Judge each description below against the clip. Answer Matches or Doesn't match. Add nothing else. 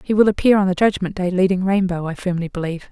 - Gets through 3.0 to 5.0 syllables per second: Doesn't match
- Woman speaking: Matches